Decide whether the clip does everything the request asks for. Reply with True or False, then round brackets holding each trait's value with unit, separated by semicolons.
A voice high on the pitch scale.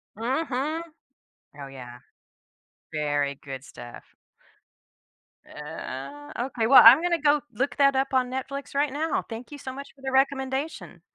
True (260 Hz)